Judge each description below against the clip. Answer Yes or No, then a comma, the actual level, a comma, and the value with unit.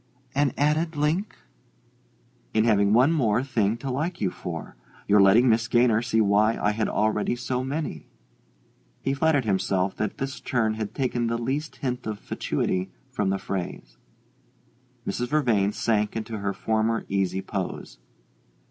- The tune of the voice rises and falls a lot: No, average, 4.4 semitones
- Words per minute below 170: Yes, average, 150 wpm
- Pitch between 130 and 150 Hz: No, low, 115 Hz